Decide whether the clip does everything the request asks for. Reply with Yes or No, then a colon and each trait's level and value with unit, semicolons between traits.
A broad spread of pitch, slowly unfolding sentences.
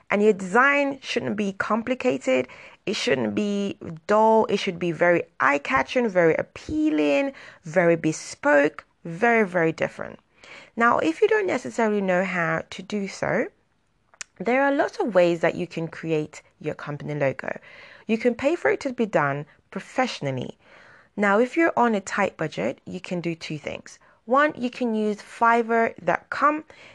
No: wide, 6.6 semitones; average, 160 wpm